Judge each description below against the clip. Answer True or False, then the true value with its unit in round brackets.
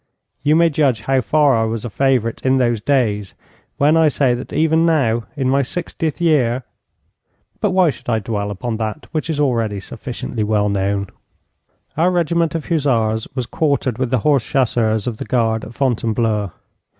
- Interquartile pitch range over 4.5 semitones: True (5.0 semitones)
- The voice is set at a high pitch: False (125 Hz)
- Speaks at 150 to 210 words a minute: True (175 wpm)